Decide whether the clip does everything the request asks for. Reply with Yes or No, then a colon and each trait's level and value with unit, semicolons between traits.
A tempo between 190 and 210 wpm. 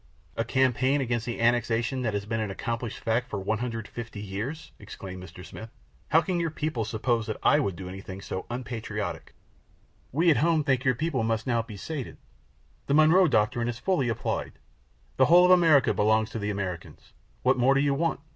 Yes: average, 195 wpm